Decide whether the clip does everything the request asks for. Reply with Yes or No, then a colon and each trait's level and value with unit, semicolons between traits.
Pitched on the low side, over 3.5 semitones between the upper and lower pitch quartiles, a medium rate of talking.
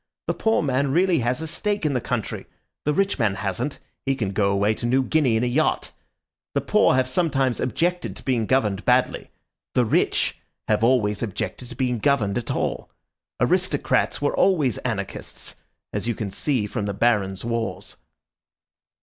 Yes: low, 125 Hz; average, 4.8 semitones; average, 175 wpm